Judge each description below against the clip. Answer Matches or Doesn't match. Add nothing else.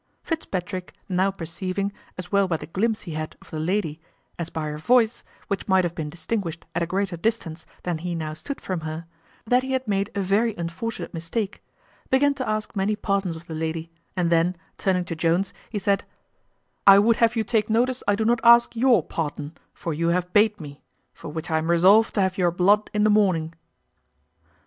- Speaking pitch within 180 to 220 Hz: Matches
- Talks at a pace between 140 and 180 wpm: Doesn't match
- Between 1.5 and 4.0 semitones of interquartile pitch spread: Doesn't match